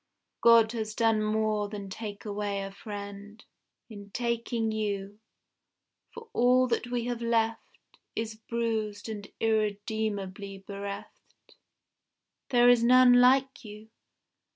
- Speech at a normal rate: No, slow, 115 wpm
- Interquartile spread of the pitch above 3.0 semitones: No, narrow, 2.4 semitones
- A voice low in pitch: No, high, 220 Hz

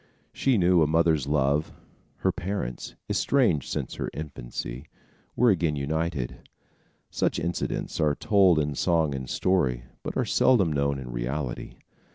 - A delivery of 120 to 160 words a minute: Yes, average, 140 wpm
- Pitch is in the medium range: No, very low, 75 Hz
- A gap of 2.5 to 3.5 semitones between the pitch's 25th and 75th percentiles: No, average, 4.0 semitones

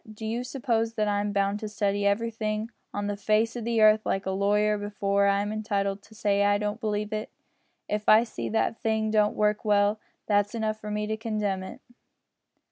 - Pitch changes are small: Yes, narrow, 1.3 semitones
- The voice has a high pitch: Yes, high, 210 Hz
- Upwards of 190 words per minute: Yes, fast, 205 wpm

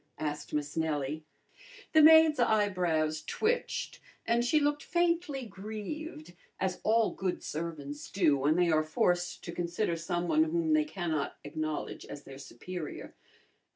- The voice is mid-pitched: Yes, medium, 175 Hz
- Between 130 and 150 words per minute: Yes, slow, 135 wpm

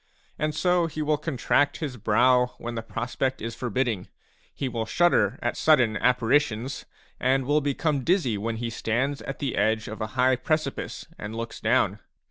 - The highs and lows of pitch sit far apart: No, average, 4.1 semitones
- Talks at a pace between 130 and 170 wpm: Yes, average, 165 wpm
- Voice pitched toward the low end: Yes, low, 125 Hz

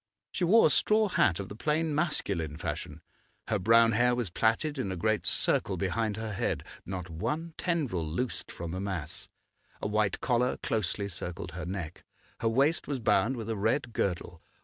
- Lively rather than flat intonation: Yes, wide, 5.7 semitones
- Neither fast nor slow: Yes, average, 180 wpm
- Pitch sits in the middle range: No, low, 110 Hz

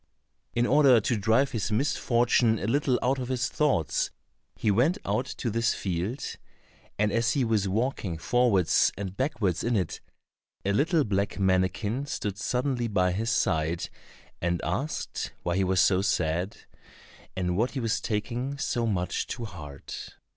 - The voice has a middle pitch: No, low, 110 Hz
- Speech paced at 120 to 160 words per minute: Yes, average, 155 wpm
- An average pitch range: Yes, average, 4.9 semitones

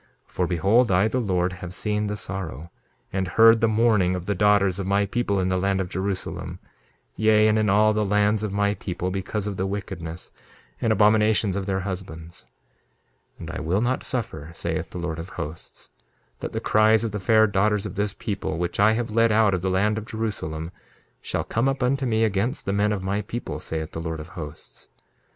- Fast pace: Yes, fast, 215 wpm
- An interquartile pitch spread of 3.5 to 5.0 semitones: No, average, 2.9 semitones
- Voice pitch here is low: Yes, low, 100 Hz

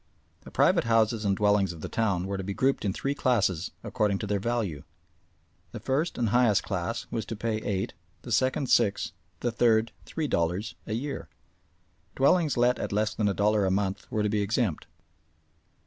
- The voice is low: Yes, low, 110 Hz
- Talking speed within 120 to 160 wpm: No, average, 190 wpm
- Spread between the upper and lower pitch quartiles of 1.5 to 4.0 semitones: Yes, average, 3.5 semitones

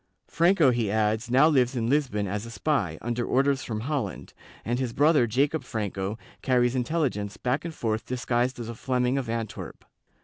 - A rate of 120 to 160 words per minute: No, average, 175 wpm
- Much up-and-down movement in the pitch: No, average, 3.6 semitones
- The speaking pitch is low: Yes, low, 125 Hz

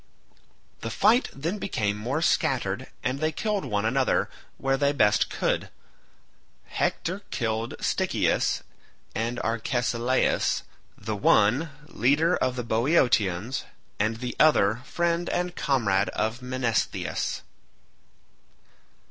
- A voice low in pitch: Yes, low, 125 Hz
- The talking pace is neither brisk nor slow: No, slow, 105 wpm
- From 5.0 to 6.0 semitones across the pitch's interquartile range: Yes, wide, 5.6 semitones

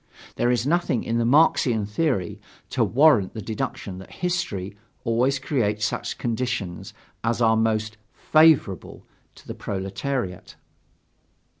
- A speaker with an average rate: No, slow, 125 wpm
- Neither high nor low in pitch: No, low, 115 Hz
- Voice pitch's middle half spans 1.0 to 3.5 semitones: No, average, 4.6 semitones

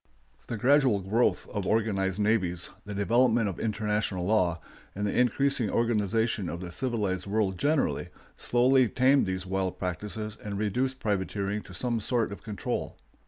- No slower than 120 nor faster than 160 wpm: Yes, average, 155 wpm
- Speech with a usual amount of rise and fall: Yes, average, 3.6 semitones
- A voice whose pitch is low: Yes, low, 105 Hz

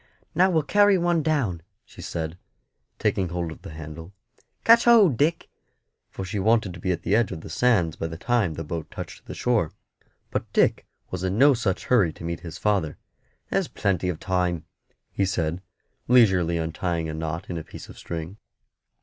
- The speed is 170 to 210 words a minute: Yes, average, 190 wpm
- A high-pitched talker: No, very low, 90 Hz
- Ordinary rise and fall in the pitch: No, wide, 6.4 semitones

